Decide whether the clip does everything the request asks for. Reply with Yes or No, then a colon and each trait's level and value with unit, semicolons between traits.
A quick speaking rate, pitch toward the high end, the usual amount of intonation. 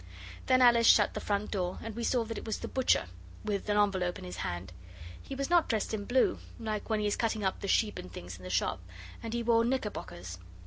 Yes: fast, 240 wpm; high, 210 Hz; average, 4.6 semitones